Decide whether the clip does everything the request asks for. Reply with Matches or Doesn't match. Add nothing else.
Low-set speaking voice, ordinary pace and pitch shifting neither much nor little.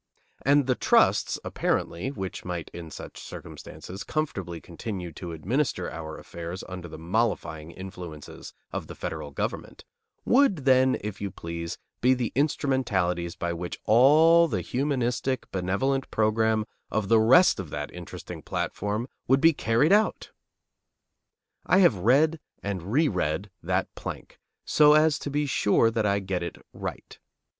Doesn't match